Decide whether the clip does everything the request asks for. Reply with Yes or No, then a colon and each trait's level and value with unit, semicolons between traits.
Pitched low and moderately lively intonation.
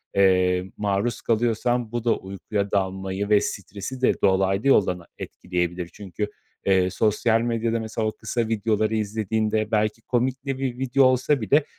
Yes: low, 110 Hz; average, 3.4 semitones